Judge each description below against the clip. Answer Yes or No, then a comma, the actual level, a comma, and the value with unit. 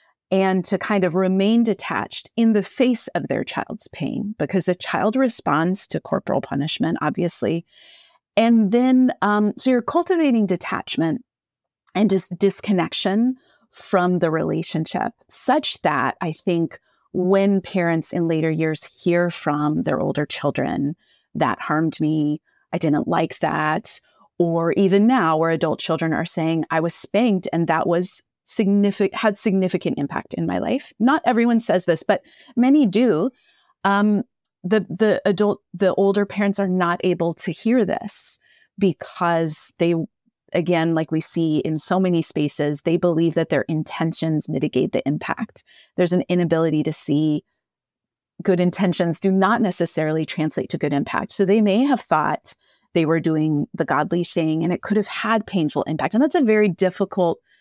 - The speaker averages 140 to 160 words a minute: Yes, average, 155 wpm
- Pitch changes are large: No, average, 4.6 semitones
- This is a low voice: No, medium, 185 Hz